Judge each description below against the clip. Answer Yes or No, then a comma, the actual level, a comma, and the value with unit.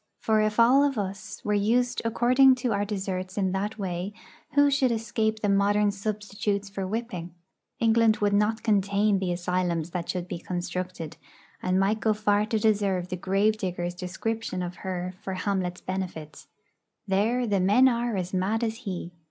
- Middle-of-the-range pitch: No, high, 200 Hz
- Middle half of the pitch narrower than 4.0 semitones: Yes, average, 3.1 semitones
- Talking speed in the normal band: Yes, average, 170 wpm